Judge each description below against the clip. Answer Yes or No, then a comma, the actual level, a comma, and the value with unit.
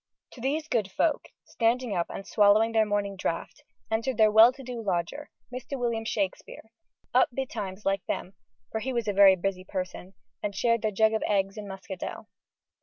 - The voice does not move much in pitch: No, average, 3.4 semitones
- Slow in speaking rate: No, average, 180 wpm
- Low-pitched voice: No, high, 215 Hz